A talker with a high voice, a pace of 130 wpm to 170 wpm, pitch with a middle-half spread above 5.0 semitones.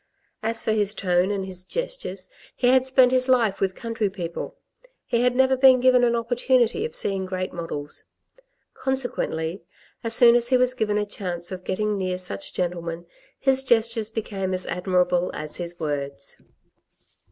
Yes: high, 210 Hz; average, 165 wpm; wide, 5.4 semitones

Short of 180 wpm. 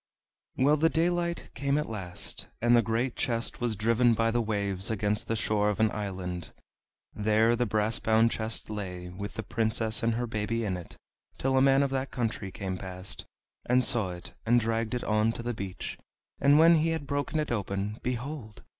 No: average, 195 wpm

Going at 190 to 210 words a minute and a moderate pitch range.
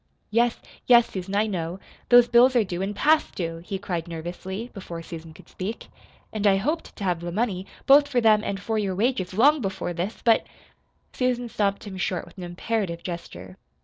Yes: average, 200 wpm; average, 4.8 semitones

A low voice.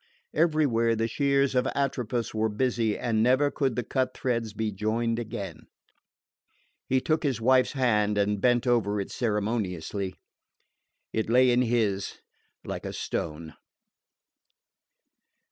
Yes: low, 115 Hz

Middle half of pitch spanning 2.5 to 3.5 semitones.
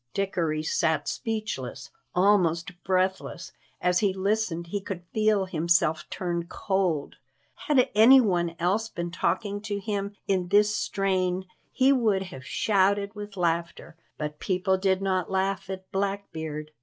Yes: average, 2.9 semitones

